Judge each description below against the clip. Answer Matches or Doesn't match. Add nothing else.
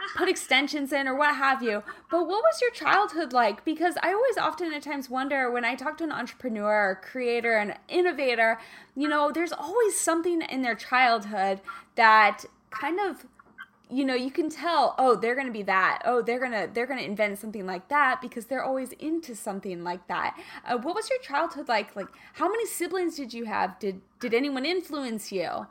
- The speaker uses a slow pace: Doesn't match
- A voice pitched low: Doesn't match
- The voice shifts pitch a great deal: Matches